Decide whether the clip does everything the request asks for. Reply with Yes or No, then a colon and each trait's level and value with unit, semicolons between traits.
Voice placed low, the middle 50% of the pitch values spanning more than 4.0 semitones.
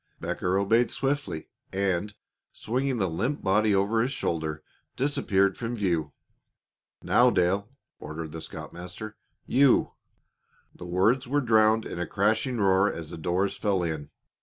Yes: low, 100 Hz; average, 4.6 semitones